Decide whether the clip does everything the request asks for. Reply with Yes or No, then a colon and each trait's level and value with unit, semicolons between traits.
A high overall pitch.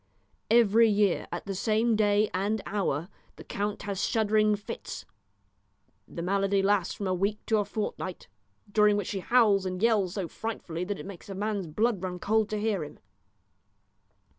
Yes: high, 205 Hz